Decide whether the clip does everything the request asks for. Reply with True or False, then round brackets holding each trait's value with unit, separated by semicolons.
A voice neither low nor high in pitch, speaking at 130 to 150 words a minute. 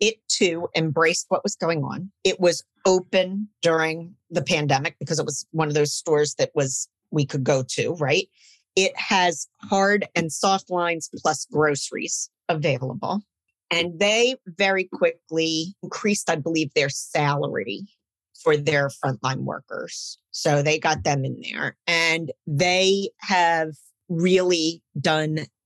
True (165 Hz; 140 wpm)